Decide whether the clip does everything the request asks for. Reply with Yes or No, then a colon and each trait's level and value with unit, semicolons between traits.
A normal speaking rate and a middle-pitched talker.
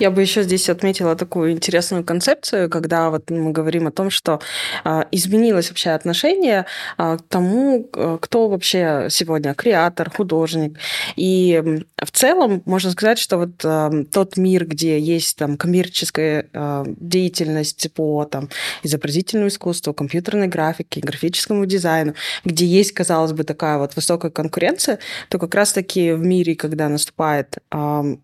Yes: average, 145 wpm; medium, 170 Hz